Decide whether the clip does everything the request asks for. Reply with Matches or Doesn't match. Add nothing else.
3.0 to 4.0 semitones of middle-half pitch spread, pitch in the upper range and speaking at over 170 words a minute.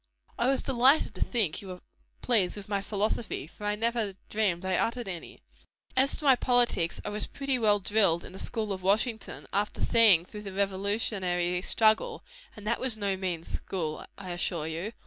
Matches